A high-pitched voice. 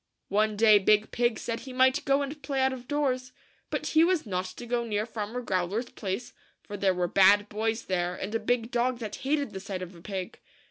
Yes: high, 225 Hz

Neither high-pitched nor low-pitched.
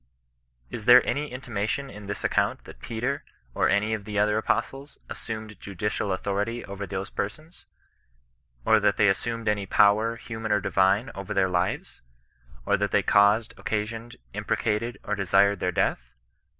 No: low, 105 Hz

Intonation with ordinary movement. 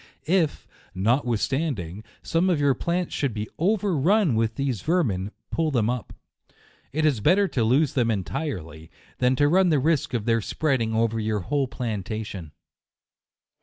No: wide, 6.2 semitones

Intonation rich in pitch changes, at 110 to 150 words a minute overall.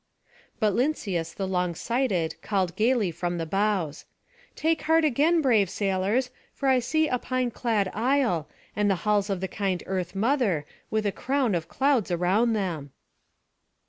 No: wide, 5.7 semitones; average, 160 wpm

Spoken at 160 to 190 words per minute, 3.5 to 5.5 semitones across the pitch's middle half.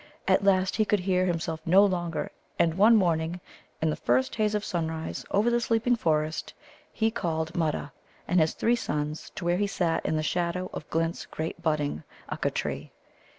Yes: average, 185 wpm; average, 3.8 semitones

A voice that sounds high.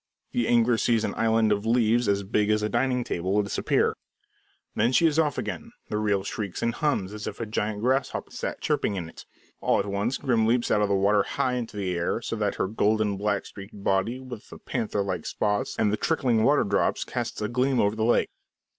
No: low, 110 Hz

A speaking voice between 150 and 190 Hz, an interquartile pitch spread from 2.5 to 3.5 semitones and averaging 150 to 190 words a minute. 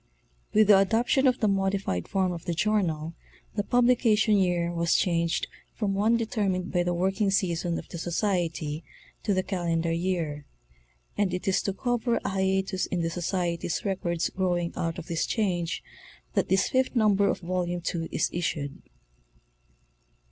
Yes: medium, 185 Hz; average, 3.1 semitones; average, 165 wpm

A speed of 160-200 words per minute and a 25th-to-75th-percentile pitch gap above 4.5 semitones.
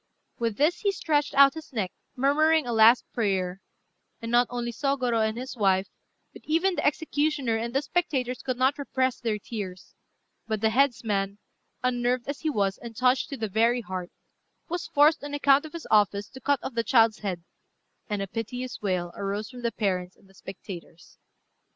Yes: average, 190 wpm; average, 5.1 semitones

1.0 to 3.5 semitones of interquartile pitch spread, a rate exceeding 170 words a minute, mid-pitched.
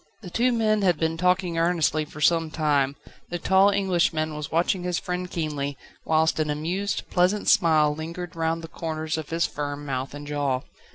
Yes: average, 2.9 semitones; average, 180 wpm; medium, 165 Hz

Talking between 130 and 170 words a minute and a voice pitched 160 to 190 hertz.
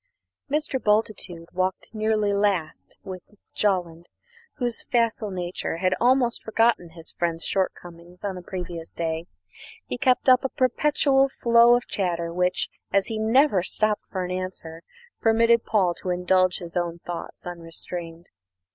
Yes: average, 140 wpm; medium, 185 Hz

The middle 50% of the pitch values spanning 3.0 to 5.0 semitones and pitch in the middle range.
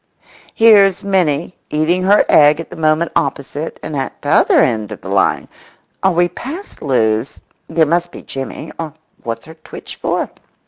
Yes: average, 4.0 semitones; medium, 160 Hz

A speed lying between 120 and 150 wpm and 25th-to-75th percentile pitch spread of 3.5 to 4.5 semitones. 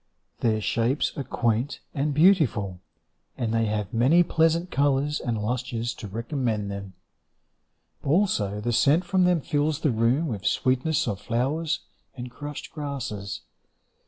No: slow, 135 wpm; average, 5.1 semitones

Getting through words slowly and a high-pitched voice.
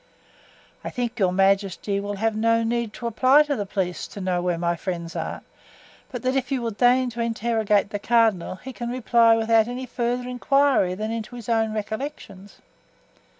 No: average, 185 wpm; high, 225 Hz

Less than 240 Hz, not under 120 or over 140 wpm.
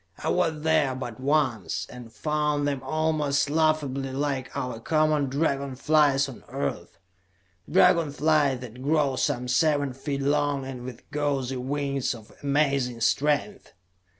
Yes: medium, 140 Hz; slow, 135 wpm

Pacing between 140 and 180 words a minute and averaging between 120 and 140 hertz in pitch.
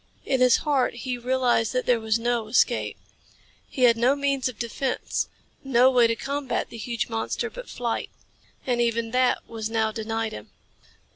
No: average, 170 wpm; high, 240 Hz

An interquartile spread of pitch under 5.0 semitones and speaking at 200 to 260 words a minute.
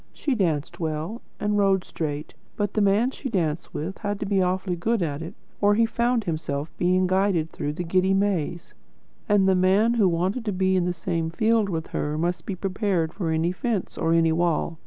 Yes: average, 3.7 semitones; fast, 205 wpm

